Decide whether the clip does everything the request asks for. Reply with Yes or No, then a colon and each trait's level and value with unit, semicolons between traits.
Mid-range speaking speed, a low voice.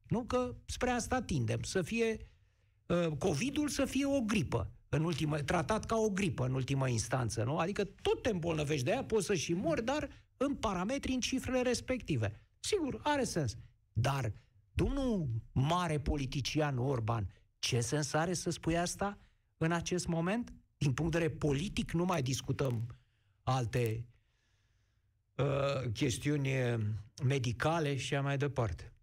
No: average, 145 wpm; medium, 150 Hz